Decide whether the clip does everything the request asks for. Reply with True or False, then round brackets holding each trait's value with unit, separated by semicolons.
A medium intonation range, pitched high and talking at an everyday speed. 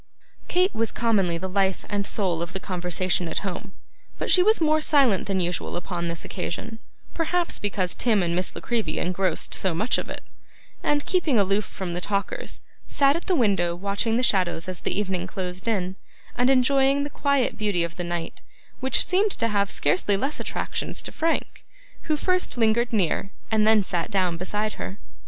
False (5.7 semitones; 200 Hz; 190 wpm)